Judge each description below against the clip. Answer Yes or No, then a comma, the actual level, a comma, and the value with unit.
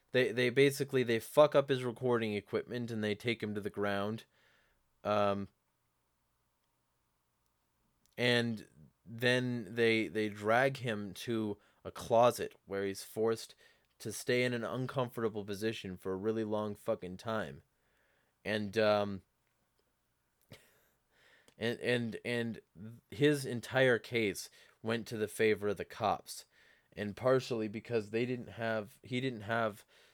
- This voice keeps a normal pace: No, slow, 130 wpm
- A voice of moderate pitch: No, low, 110 Hz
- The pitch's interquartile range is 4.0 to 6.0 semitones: No, average, 2.8 semitones